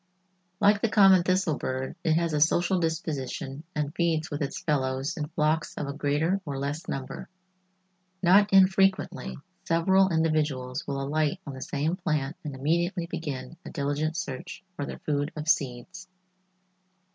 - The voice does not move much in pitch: No, average, 3.6 semitones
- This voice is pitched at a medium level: Yes, medium, 155 Hz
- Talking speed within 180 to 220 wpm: No, average, 155 wpm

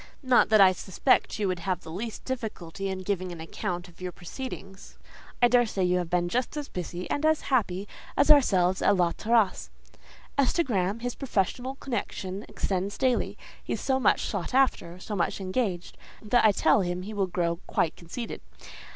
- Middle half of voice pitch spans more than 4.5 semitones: Yes, average, 5.2 semitones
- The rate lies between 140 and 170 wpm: No, average, 185 wpm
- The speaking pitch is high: Yes, high, 195 Hz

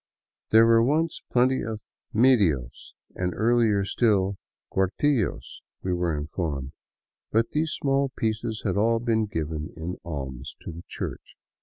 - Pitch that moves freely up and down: Yes, wide, 5.7 semitones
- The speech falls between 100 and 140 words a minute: Yes, slow, 135 wpm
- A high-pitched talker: No, low, 105 Hz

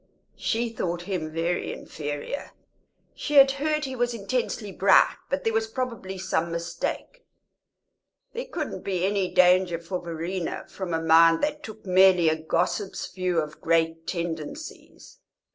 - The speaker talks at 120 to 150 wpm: Yes, average, 145 wpm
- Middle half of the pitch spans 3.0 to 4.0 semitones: No, wide, 5.4 semitones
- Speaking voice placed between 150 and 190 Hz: Yes, medium, 185 Hz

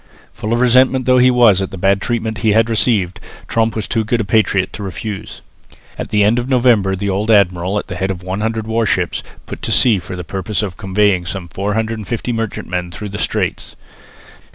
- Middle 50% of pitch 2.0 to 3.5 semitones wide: Yes, average, 2.8 semitones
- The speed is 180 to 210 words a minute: Yes, average, 200 wpm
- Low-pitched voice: Yes, low, 105 Hz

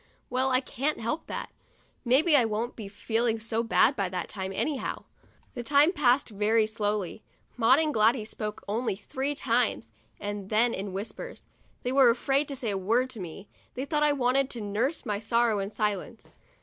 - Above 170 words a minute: Yes, average, 185 wpm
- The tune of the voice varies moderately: Yes, average, 4.0 semitones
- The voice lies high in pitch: Yes, high, 230 Hz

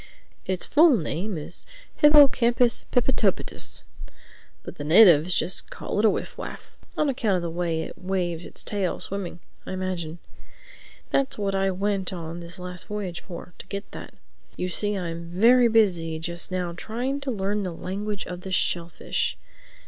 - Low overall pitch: No, medium, 185 Hz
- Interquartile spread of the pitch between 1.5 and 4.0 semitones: Yes, average, 3.5 semitones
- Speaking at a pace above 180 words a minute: No, average, 160 wpm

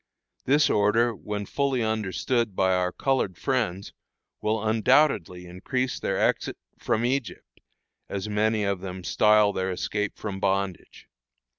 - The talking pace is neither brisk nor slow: No, slow, 130 wpm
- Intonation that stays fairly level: No, average, 3.7 semitones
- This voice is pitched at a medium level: No, low, 105 Hz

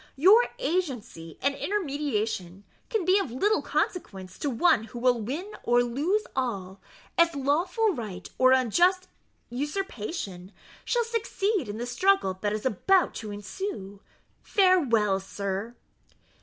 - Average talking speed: No, slow, 130 wpm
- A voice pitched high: Yes, very high, 260 Hz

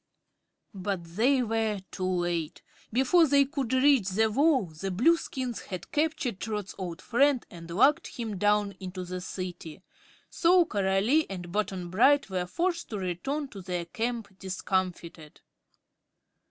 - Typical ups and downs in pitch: No, wide, 6.2 semitones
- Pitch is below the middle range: No, high, 205 Hz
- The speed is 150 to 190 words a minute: No, average, 140 wpm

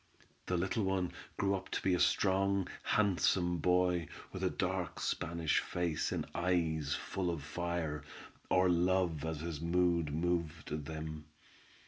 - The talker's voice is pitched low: Yes, very low, 85 Hz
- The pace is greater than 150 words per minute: No, slow, 135 wpm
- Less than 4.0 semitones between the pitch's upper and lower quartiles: Yes, narrow, 2.4 semitones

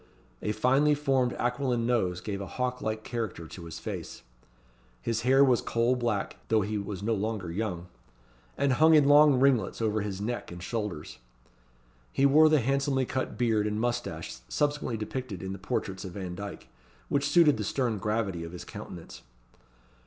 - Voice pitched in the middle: No, low, 115 Hz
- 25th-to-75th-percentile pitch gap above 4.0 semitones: Yes, average, 4.9 semitones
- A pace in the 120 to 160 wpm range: No, average, 170 wpm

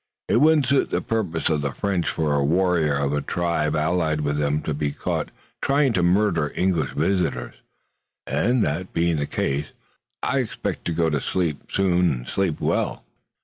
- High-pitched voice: No, very low, 85 Hz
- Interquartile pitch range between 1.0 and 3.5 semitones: No, average, 4.0 semitones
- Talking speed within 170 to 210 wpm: Yes, average, 180 wpm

